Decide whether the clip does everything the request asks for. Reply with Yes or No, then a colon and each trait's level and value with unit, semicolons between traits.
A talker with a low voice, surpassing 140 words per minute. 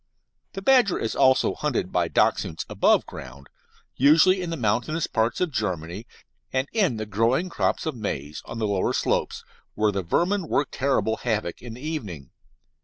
Yes: low, 115 Hz; average, 170 wpm